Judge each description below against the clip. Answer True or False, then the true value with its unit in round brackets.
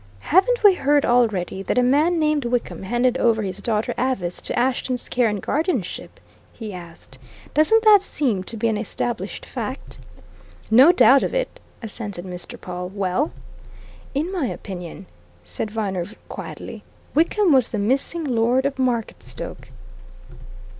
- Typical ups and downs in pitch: False (6.3 semitones)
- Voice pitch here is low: False (240 Hz)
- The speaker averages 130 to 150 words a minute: True (145 wpm)